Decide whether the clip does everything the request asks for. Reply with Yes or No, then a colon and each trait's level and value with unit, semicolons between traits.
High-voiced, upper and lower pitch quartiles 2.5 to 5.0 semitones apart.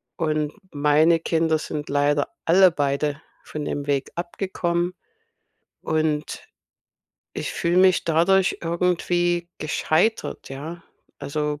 No: medium, 160 Hz; average, 2.8 semitones